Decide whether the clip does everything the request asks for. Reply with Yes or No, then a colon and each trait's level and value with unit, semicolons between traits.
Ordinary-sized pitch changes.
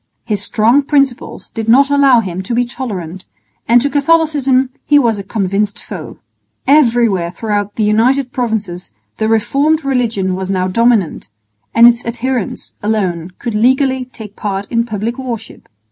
Yes: average, 4.2 semitones